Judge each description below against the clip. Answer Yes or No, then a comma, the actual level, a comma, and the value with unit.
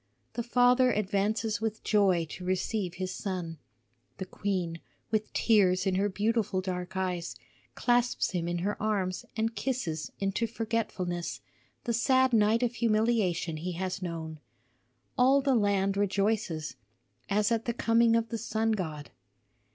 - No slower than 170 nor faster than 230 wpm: No, average, 145 wpm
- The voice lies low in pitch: No, high, 205 Hz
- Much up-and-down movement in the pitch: No, average, 3.8 semitones